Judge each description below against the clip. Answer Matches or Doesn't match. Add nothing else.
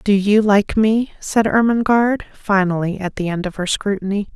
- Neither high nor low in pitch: Doesn't match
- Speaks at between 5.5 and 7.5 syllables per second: Doesn't match